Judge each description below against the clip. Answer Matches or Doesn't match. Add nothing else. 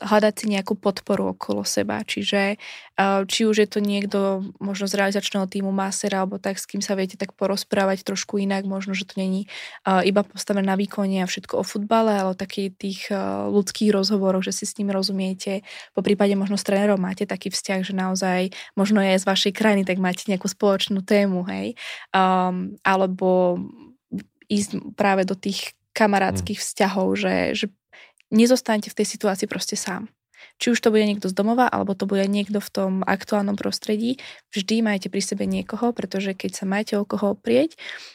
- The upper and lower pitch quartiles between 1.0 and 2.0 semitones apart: Matches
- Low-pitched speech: Doesn't match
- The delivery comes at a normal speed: Doesn't match